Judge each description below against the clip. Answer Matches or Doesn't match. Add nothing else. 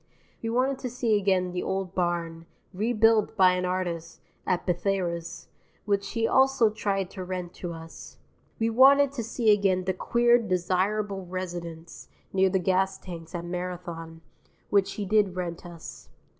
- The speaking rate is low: Doesn't match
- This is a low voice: Doesn't match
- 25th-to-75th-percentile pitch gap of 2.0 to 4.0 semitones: Matches